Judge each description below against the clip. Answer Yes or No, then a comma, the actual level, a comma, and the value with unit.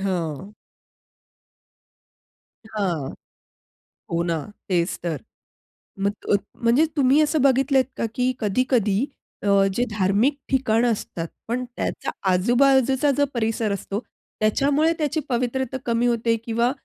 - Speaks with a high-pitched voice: Yes, high, 235 Hz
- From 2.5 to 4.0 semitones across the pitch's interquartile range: No, average, 4.7 semitones